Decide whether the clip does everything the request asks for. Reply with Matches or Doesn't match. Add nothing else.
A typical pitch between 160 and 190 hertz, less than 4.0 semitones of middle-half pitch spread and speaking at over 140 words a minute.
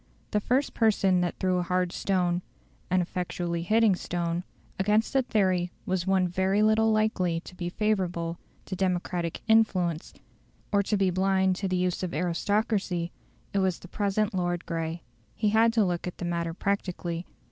Matches